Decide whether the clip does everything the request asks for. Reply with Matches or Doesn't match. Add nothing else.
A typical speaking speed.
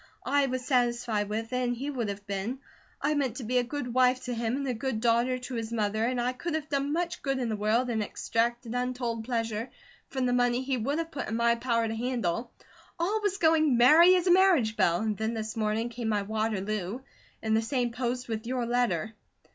Doesn't match